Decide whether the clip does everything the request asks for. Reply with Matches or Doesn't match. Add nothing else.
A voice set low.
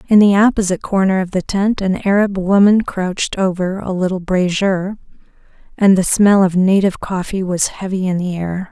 Doesn't match